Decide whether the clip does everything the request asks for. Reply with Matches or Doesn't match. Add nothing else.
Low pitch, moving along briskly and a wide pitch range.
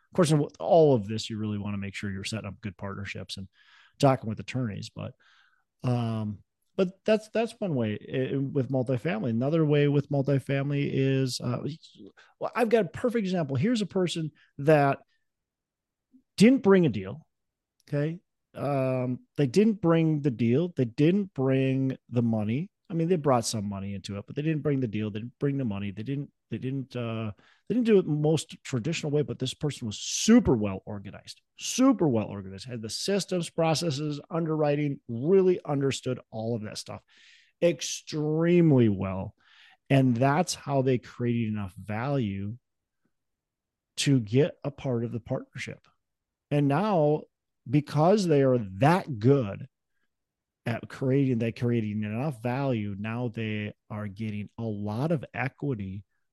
Doesn't match